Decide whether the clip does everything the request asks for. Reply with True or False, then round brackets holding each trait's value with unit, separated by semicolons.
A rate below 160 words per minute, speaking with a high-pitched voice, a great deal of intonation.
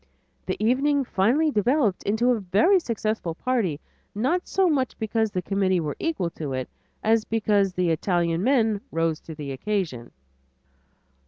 True (150 wpm; 210 Hz; 6.1 semitones)